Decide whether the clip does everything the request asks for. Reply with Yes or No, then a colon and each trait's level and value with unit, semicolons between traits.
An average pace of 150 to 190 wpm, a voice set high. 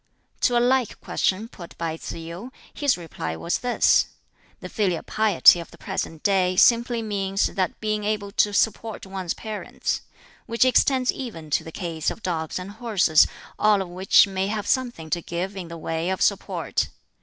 Yes: average, 180 wpm; high, 195 Hz